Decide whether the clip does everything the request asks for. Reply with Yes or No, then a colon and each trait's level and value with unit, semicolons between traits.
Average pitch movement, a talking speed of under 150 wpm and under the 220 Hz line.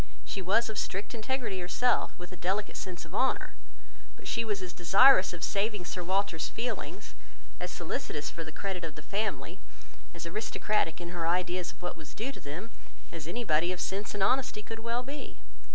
No: average, 4.0 semitones; average, 190 wpm; high, 190 Hz